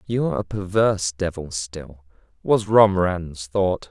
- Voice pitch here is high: No, very low, 90 Hz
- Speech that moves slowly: Yes, slow, 125 wpm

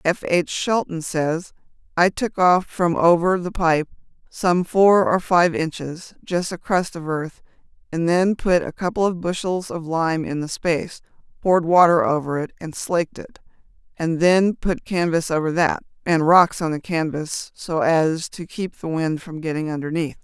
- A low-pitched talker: No, medium, 170 Hz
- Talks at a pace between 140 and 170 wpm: No, average, 180 wpm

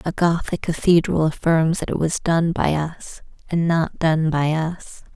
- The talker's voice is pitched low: No, medium, 165 Hz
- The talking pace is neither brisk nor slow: Yes, average, 175 wpm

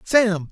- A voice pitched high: Yes, high, 200 Hz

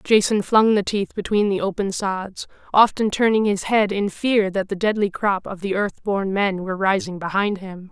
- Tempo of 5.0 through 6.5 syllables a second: No, 4.8 syllables/s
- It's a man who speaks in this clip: No, female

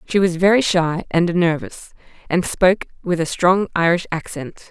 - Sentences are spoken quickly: No, average, 165 wpm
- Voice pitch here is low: No, medium, 175 Hz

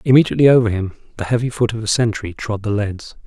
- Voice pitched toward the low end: Yes, low, 110 Hz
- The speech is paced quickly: Yes, fast, 220 wpm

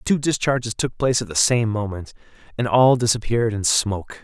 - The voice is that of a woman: No, male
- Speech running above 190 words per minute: Yes, average, 200 wpm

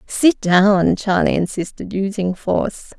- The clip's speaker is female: Yes, female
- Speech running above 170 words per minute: No, slow, 120 wpm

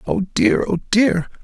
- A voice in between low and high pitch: Yes, medium, 155 Hz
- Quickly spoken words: No, average, 170 wpm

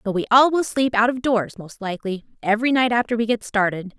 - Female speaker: Yes, female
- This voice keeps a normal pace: No, fast, 240 wpm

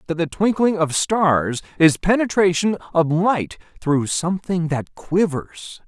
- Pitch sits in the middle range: Yes, medium, 170 Hz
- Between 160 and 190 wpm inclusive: No, slow, 135 wpm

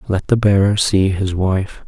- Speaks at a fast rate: No, average, 190 wpm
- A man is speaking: Yes, male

